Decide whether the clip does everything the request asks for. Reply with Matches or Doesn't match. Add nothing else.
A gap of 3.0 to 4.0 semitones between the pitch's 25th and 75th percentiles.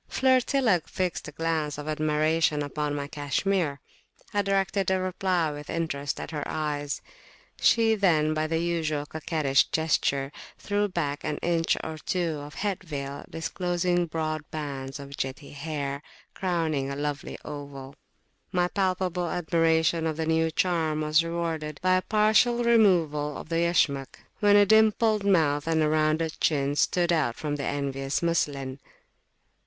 Matches